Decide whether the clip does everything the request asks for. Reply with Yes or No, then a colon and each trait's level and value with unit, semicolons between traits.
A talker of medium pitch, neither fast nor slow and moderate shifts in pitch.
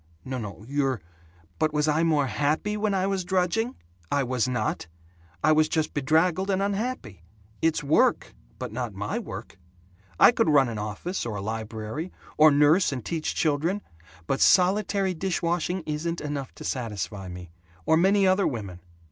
No: medium, 150 Hz; average, 170 wpm; wide, 6.9 semitones